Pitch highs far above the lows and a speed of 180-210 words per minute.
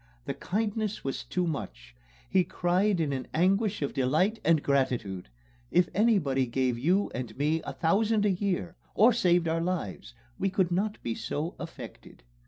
No: wide, 6.4 semitones; average, 165 wpm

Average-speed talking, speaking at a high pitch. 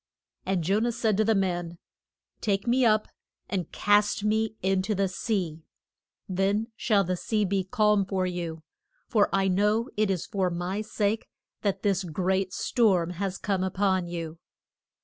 Yes: average, 170 wpm; high, 195 Hz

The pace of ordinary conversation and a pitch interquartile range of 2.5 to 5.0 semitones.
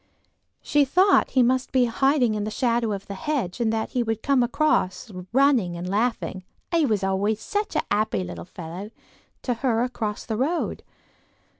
Yes: average, 160 wpm; average, 4.2 semitones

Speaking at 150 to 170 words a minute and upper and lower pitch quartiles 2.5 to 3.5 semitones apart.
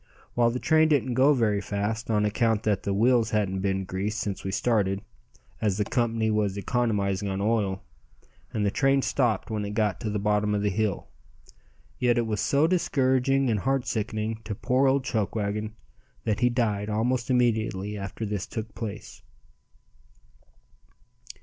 Yes: average, 165 wpm; average, 3.0 semitones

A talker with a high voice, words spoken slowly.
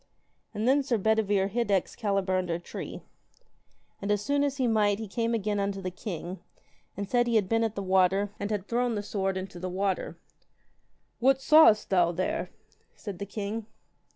No: high, 205 Hz; average, 185 wpm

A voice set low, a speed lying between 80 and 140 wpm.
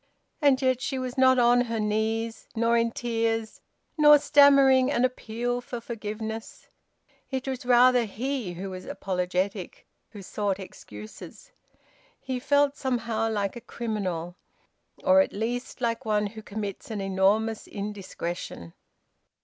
No: high, 225 Hz; slow, 135 wpm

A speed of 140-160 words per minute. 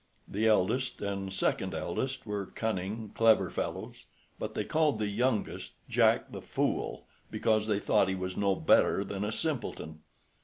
Yes: average, 155 wpm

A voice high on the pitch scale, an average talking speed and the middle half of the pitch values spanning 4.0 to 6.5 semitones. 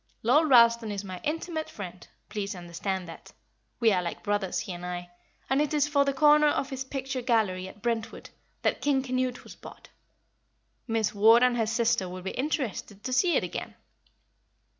Yes: high, 230 Hz; average, 185 wpm; wide, 5.6 semitones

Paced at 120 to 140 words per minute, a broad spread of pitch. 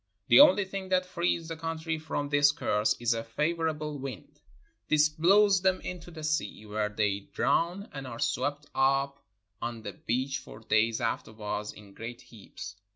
No: average, 175 wpm; wide, 6.5 semitones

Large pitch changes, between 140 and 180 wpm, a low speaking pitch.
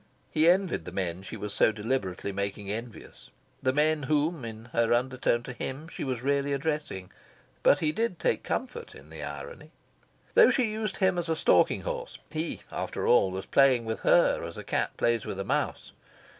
No: wide, 7.2 semitones; average, 190 wpm; low, 130 Hz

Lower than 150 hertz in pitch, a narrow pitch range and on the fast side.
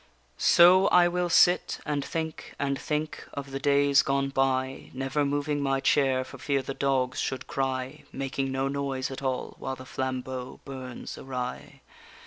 No: low, 135 Hz; narrow, 1.4 semitones; average, 165 wpm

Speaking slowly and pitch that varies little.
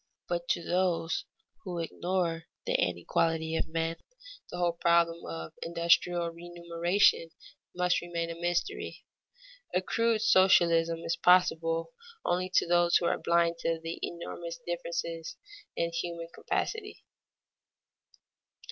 Yes: slow, 120 wpm; narrow, 1.0 semitones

